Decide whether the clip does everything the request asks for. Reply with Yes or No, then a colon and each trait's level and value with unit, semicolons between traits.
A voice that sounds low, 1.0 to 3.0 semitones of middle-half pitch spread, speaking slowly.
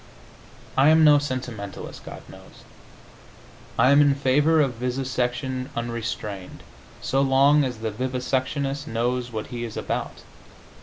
Yes: low, 130 Hz; average, 2.7 semitones; slow, 125 wpm